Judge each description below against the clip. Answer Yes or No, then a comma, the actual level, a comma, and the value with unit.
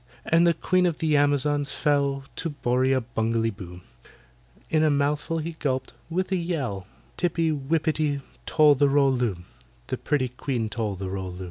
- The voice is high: No, medium, 140 Hz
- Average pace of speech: Yes, average, 165 wpm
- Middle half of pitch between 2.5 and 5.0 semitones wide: Yes, average, 4.5 semitones